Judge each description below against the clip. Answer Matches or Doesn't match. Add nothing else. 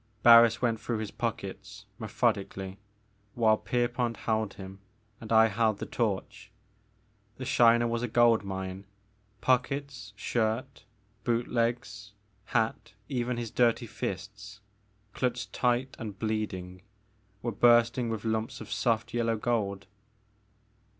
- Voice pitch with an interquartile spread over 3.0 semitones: Doesn't match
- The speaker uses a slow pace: Matches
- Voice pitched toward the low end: Matches